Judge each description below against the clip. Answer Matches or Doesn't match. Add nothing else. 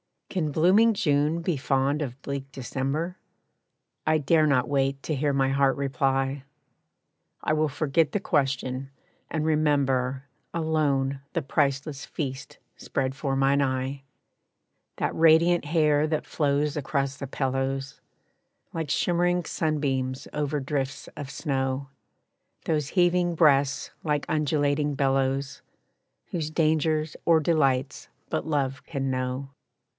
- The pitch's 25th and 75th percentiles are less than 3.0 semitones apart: Matches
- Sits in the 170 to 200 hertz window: Doesn't match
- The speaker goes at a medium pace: Doesn't match